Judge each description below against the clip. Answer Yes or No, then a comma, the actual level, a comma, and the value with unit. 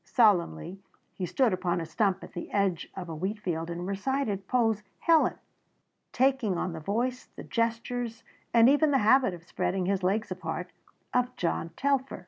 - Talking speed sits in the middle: Yes, average, 165 wpm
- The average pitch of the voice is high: Yes, high, 200 Hz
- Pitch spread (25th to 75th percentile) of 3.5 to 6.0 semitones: Yes, wide, 5.5 semitones